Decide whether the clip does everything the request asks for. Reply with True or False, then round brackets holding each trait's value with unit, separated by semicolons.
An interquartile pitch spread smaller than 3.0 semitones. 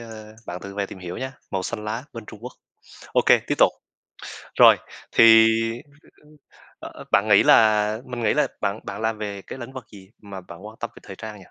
True (2.4 semitones)